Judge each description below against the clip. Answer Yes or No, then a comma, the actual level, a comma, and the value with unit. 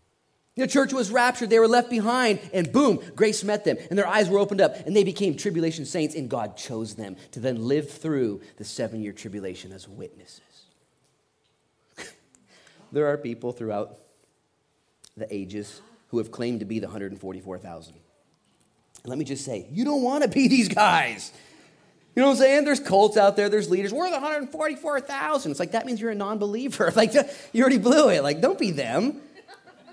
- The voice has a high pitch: Yes, high, 200 Hz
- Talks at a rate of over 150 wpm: Yes, average, 185 wpm